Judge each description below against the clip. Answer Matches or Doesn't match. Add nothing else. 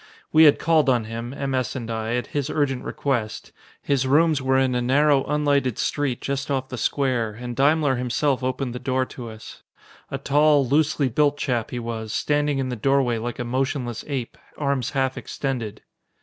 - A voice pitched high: Doesn't match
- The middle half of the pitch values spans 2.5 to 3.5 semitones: Matches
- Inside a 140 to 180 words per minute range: Doesn't match